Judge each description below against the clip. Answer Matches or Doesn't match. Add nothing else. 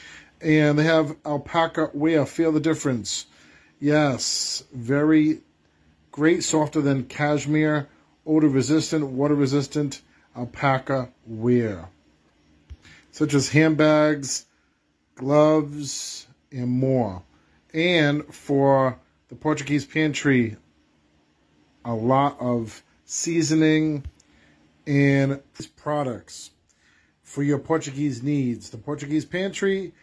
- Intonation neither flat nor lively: Matches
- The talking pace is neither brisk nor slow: Doesn't match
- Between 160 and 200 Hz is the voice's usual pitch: Doesn't match